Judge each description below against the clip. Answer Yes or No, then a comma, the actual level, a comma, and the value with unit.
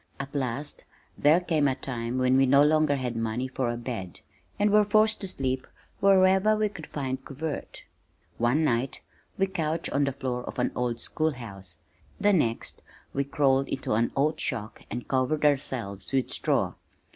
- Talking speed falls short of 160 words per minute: No, average, 175 wpm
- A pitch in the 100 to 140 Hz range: Yes, low, 135 Hz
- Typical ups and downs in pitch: Yes, average, 4.2 semitones